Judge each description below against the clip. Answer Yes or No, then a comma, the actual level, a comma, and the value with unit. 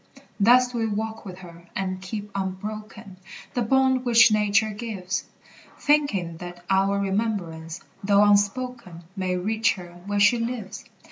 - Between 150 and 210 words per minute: No, average, 140 wpm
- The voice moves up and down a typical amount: Yes, average, 3.3 semitones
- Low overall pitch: No, high, 205 Hz